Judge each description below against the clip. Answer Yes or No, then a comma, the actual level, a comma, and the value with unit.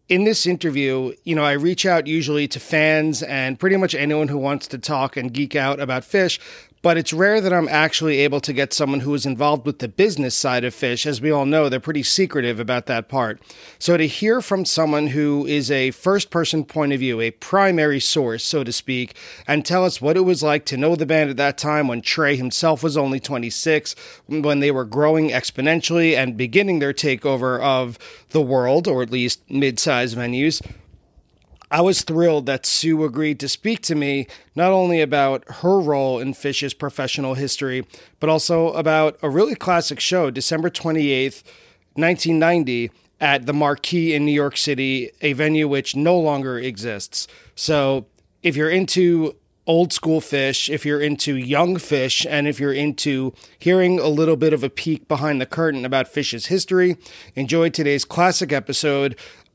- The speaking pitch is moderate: Yes, medium, 150 Hz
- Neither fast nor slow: Yes, average, 190 wpm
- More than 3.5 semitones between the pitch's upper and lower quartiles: No, average, 3.2 semitones